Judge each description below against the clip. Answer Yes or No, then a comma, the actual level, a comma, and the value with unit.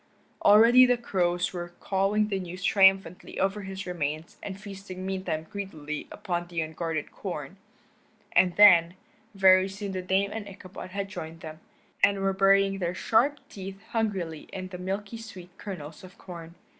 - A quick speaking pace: No, average, 155 wpm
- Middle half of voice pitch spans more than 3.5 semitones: No, narrow, 2.4 semitones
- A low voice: No, high, 190 Hz